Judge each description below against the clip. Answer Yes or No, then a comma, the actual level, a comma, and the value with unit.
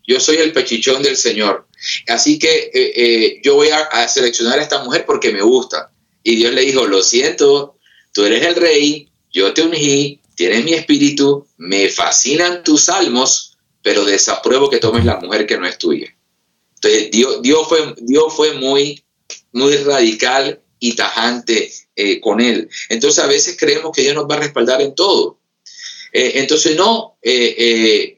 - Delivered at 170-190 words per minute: Yes, average, 175 wpm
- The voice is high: Yes, very high, 370 Hz